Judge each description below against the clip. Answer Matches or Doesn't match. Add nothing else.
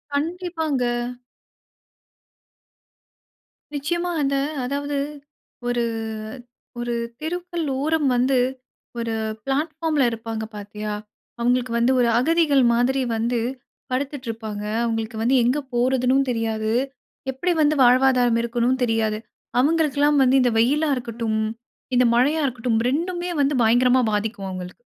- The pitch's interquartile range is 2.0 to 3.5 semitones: Doesn't match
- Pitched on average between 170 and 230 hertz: Doesn't match